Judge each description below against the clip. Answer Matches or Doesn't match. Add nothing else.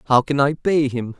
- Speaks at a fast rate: Matches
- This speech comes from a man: Matches